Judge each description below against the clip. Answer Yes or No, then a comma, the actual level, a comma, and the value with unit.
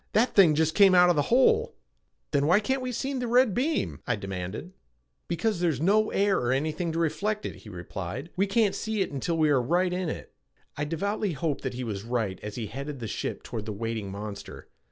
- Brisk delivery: Yes, fast, 220 wpm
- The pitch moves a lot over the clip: Yes, wide, 8.9 semitones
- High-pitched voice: No, medium, 160 Hz